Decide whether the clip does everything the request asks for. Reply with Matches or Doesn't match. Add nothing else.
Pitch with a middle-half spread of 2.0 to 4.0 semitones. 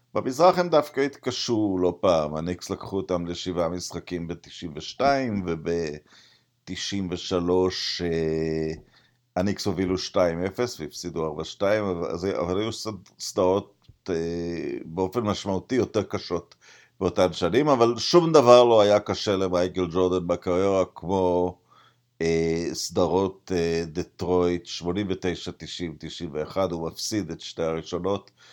Matches